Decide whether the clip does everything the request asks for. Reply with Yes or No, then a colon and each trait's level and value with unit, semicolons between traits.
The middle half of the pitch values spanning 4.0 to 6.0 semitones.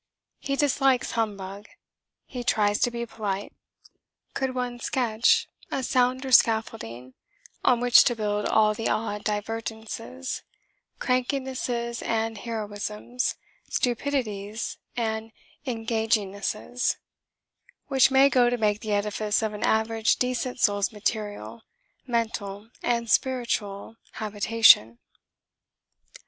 No: average, 2.8 semitones